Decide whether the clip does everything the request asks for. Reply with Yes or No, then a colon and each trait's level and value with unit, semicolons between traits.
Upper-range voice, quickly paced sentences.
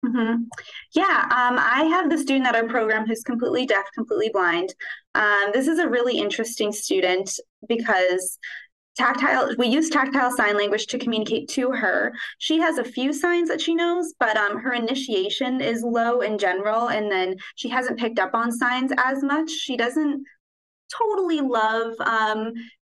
No: high, 245 Hz; average, 170 wpm